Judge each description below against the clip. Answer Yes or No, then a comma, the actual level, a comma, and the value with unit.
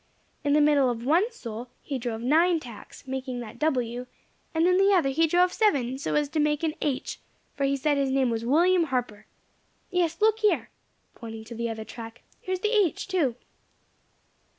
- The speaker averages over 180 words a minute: Yes, average, 195 wpm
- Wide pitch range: Yes, wide, 5.8 semitones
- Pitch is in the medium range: No, very high, 280 Hz